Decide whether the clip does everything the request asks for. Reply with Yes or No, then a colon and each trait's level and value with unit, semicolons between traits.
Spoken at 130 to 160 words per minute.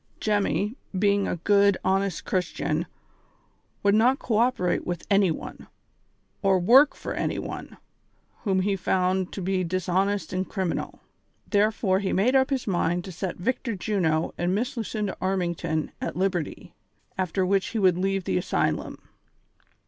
Yes: average, 150 wpm